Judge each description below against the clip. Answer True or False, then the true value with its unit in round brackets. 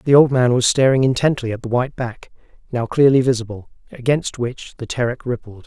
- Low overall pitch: True (125 Hz)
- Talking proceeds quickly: False (190 wpm)